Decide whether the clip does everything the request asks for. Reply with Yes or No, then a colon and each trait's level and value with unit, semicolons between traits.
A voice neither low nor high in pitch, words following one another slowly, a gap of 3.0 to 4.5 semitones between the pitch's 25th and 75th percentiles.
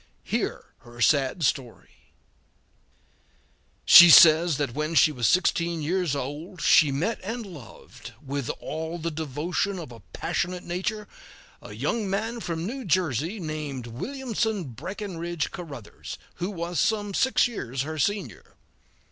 No: medium, 165 Hz; slow, 130 wpm; average, 5.1 semitones